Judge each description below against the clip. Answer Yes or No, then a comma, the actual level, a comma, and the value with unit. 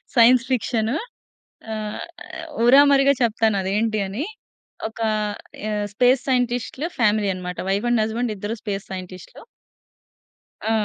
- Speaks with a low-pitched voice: No, high, 225 Hz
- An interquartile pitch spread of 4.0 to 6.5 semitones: No, average, 3.0 semitones